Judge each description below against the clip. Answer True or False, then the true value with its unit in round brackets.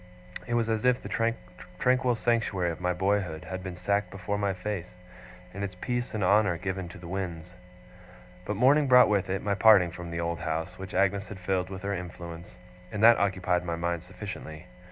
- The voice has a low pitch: True (95 Hz)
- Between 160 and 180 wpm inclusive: False (195 wpm)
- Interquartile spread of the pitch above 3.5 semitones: False (2.9 semitones)